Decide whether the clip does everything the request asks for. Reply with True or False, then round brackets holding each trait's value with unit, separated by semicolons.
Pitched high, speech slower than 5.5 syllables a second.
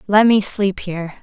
True (195 Hz; 4.9 syllables/s)